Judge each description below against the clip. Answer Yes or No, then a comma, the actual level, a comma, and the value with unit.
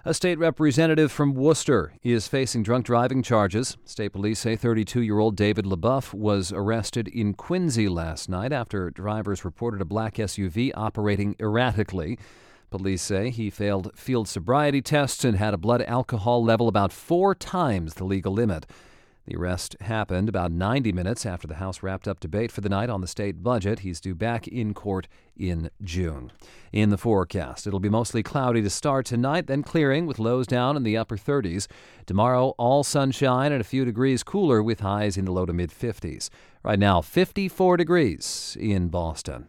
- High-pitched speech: No, low, 110 Hz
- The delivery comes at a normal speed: Yes, average, 180 wpm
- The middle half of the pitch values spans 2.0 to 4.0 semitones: No, average, 4.5 semitones